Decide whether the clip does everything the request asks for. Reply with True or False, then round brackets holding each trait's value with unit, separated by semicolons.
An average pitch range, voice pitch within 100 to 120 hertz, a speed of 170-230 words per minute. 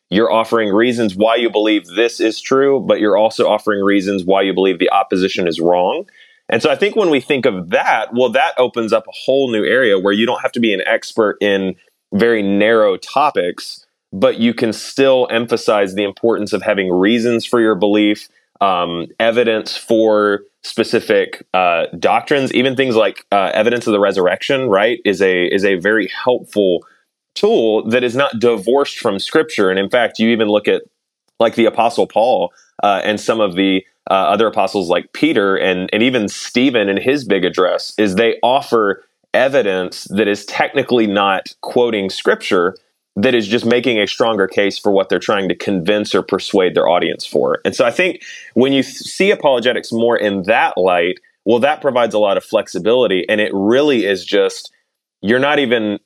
True (3.5 semitones; 110 Hz; 190 wpm)